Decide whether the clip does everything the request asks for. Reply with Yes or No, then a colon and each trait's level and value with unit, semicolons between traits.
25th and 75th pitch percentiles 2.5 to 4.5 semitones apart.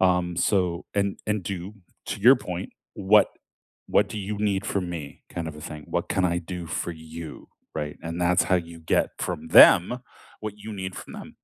Yes: average, 3.1 semitones